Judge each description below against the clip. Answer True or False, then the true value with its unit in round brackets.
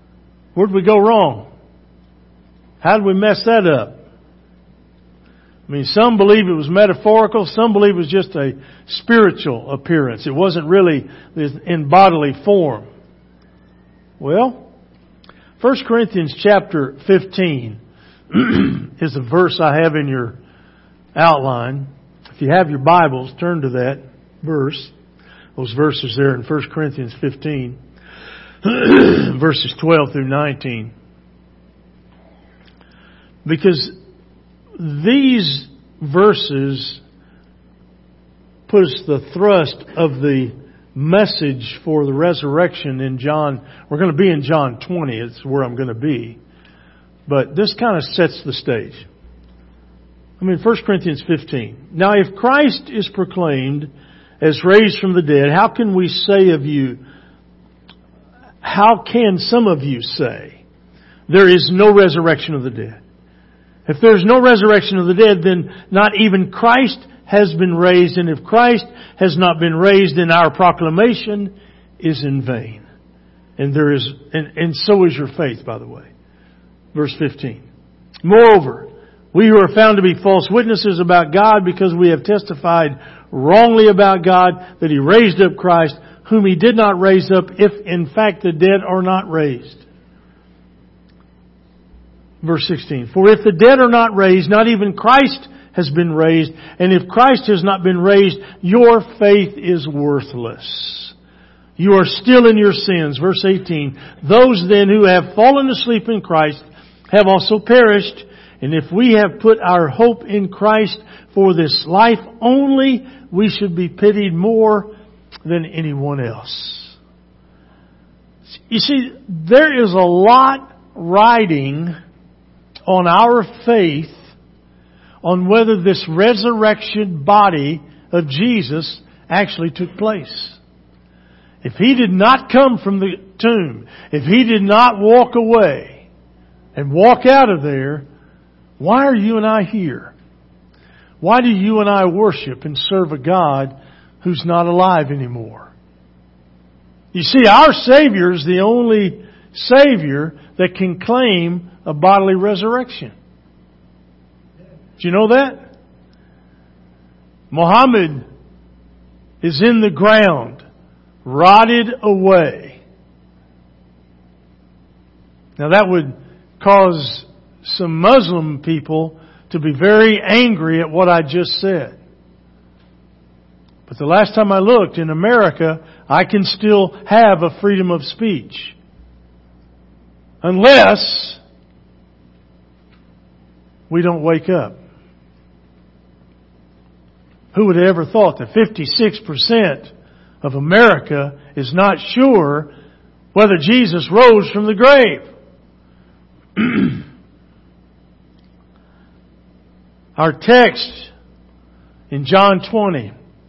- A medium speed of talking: False (125 wpm)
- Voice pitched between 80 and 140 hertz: False (165 Hz)